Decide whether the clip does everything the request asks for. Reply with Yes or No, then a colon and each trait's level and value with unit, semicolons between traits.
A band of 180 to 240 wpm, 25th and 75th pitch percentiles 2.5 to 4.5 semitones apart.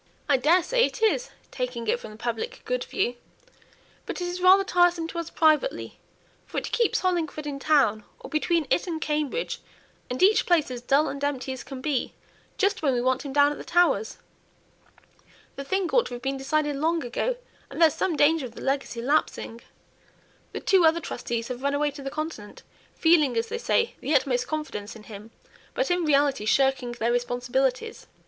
No: average, 190 wpm; average, 5.3 semitones